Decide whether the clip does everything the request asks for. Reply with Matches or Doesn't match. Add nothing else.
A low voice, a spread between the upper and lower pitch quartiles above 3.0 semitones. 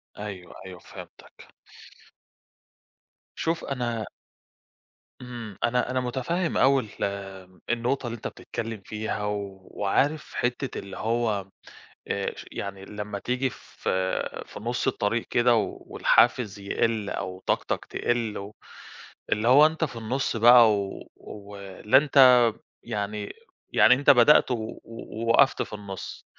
Matches